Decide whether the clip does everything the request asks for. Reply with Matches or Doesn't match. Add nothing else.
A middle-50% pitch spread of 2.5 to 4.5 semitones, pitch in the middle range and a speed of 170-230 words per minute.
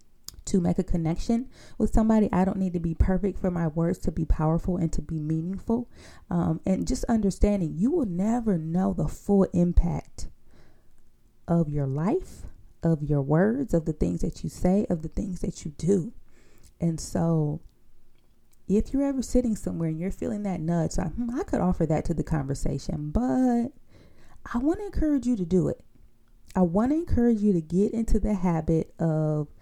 Doesn't match